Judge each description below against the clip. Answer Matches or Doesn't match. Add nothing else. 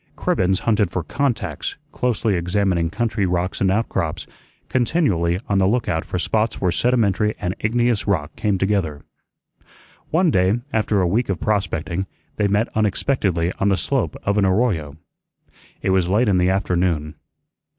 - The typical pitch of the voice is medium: Doesn't match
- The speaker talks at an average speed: Matches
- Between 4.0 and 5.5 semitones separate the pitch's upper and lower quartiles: Doesn't match